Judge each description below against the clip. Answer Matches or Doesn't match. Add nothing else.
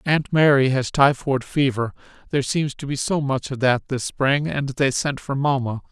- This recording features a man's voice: Matches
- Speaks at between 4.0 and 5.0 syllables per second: Matches